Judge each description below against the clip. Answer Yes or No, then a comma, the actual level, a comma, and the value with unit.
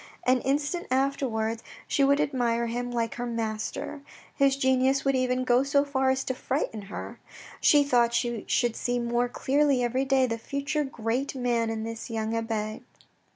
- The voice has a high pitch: Yes, very high, 250 Hz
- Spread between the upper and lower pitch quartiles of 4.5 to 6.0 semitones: No, average, 2.9 semitones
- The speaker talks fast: No, average, 175 wpm